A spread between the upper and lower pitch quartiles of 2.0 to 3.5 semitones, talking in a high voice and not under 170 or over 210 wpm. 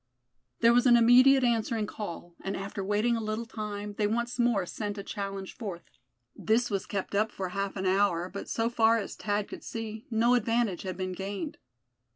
Yes: average, 2.8 semitones; high, 210 Hz; average, 195 wpm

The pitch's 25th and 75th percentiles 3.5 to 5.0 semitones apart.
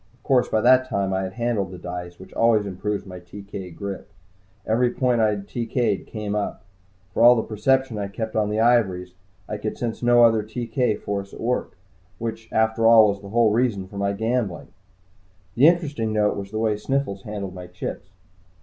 No: average, 3.0 semitones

